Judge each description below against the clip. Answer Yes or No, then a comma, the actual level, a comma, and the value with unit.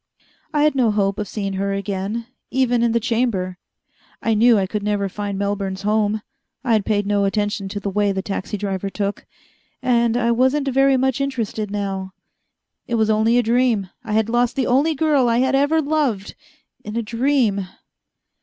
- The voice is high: Yes, high, 220 Hz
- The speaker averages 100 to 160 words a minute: No, average, 185 wpm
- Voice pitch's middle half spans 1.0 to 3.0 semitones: No, average, 3.6 semitones